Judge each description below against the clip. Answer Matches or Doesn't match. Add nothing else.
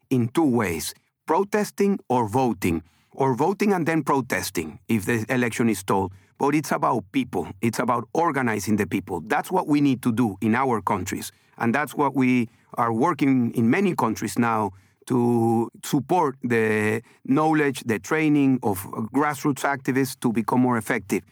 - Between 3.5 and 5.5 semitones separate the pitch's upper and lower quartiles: Matches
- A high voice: Doesn't match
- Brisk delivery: Matches